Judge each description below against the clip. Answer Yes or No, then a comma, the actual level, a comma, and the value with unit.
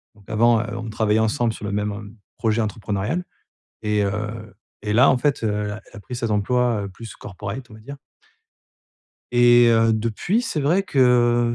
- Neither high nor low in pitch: No, low, 115 Hz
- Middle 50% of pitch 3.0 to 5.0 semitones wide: No, narrow, 2.5 semitones